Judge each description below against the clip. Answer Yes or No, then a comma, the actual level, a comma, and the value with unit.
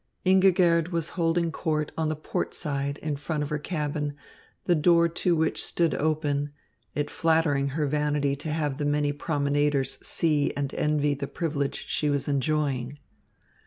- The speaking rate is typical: Yes, average, 160 wpm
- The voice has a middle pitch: Yes, medium, 150 Hz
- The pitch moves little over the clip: Yes, narrow, 2.1 semitones